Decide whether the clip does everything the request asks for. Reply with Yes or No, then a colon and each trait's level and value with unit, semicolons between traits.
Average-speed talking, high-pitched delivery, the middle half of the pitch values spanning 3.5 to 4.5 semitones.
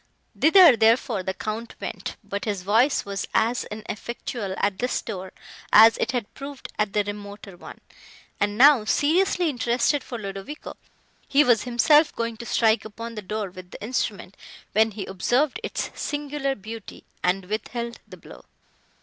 Yes: average, 160 wpm; high, 225 Hz; average, 3.8 semitones